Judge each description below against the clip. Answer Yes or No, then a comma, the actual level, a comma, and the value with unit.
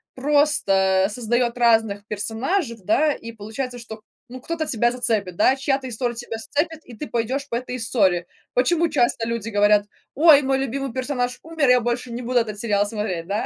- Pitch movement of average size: Yes, average, 3.7 semitones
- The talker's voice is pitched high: Yes, high, 240 Hz